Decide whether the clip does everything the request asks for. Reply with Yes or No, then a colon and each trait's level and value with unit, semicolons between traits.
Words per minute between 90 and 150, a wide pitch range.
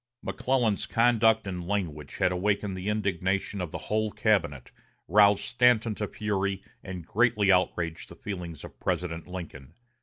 No: average, 145 wpm; average, 3.1 semitones